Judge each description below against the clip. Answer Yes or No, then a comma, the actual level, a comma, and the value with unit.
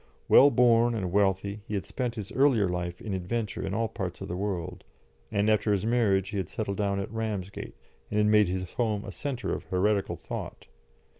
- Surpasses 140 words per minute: Yes, fast, 205 wpm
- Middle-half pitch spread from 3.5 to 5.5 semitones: No, average, 2.8 semitones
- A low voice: Yes, low, 105 Hz